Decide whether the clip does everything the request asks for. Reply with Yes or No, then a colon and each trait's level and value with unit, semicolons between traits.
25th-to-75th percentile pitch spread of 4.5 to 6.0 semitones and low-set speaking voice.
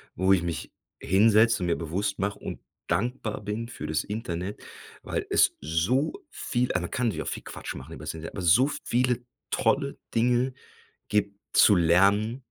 Yes: average, 5.3 semitones; low, 100 Hz